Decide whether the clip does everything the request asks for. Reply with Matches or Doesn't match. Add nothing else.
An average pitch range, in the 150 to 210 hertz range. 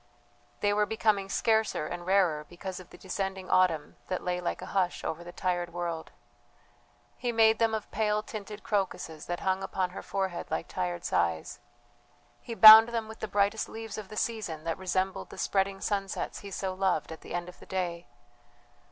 Matches